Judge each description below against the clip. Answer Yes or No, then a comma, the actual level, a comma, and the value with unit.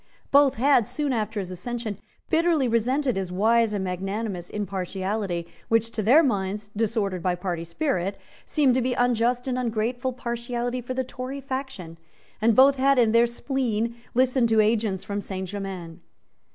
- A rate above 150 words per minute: Yes, average, 160 wpm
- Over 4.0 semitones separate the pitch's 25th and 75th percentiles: Yes, average, 4.4 semitones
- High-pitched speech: Yes, high, 230 Hz